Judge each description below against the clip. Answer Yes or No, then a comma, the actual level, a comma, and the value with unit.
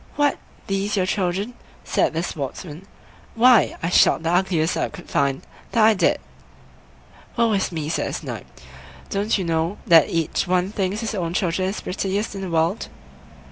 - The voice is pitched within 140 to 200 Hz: Yes, medium, 185 Hz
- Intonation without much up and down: No, average, 3.6 semitones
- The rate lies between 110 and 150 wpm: No, average, 175 wpm